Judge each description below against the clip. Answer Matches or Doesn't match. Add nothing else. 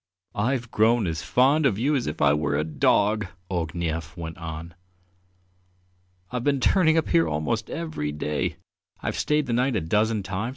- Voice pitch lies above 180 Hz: Doesn't match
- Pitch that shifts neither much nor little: Doesn't match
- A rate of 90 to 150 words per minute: Doesn't match